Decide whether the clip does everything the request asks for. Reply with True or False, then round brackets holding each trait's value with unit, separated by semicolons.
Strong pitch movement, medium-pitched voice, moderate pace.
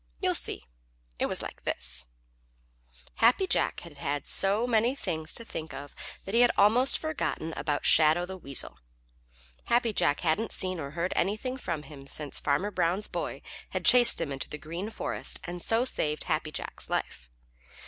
True (7.0 semitones; 175 Hz; 170 wpm)